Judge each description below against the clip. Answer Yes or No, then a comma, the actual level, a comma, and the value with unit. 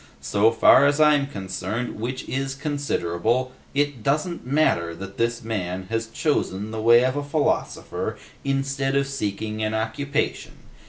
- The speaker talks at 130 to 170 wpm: Yes, average, 145 wpm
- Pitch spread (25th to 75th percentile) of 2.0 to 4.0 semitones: No, average, 4.5 semitones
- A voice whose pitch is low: Yes, low, 125 Hz